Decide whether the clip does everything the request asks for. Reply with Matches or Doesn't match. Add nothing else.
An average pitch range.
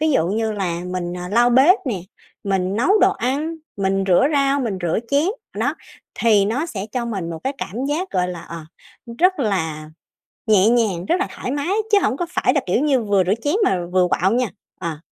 Doesn't match